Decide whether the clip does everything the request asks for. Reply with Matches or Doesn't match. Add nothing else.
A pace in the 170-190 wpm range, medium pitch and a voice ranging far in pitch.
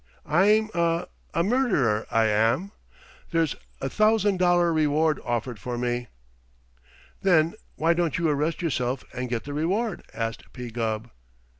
Doesn't match